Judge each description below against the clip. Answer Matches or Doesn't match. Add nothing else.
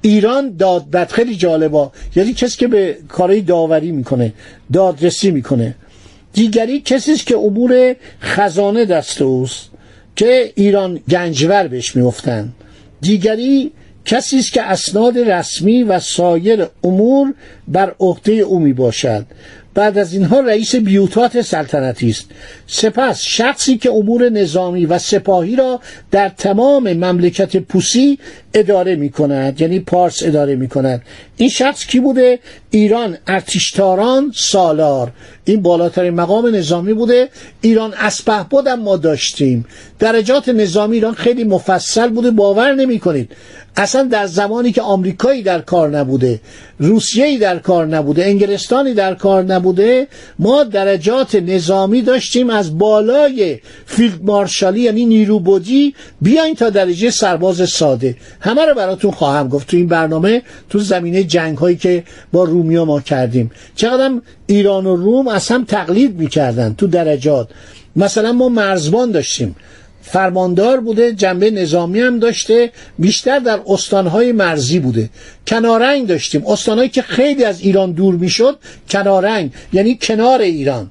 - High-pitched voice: Matches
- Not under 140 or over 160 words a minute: Doesn't match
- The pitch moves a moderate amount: Doesn't match